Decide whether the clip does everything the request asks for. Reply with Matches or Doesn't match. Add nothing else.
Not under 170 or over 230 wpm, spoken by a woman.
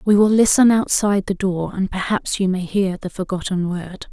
Matches